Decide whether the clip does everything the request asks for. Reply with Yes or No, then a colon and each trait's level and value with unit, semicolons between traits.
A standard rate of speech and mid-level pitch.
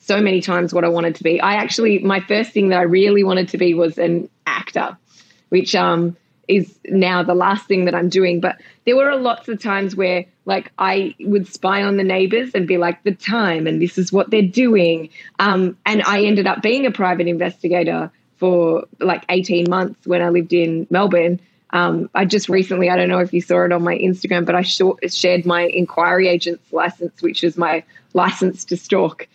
No: fast, 210 wpm; medium, 180 Hz